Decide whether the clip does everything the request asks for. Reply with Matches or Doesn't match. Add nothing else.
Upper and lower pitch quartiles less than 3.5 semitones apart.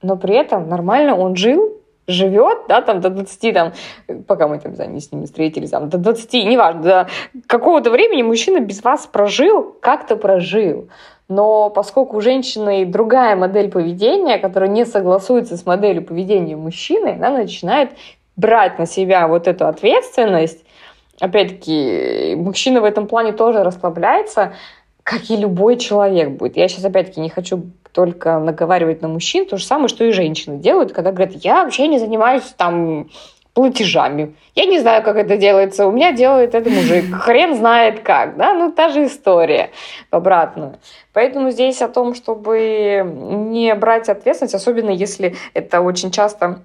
Doesn't match